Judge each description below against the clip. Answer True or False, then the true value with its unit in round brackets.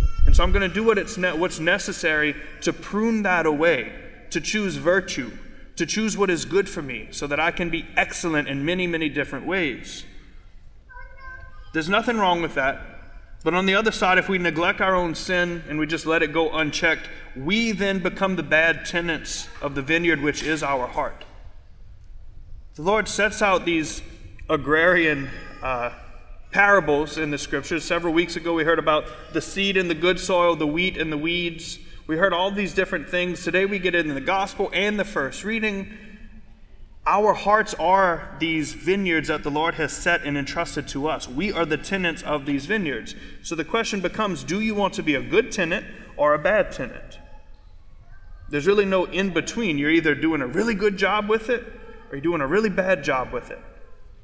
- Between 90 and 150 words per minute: False (195 wpm)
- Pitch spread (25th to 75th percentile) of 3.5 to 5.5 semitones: True (4.2 semitones)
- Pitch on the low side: False (170 Hz)